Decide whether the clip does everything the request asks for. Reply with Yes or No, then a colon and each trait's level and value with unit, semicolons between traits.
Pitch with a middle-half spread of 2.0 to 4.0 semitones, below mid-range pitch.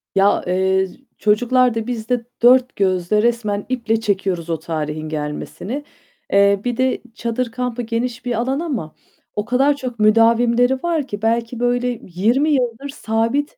No: average, 3.7 semitones; high, 230 Hz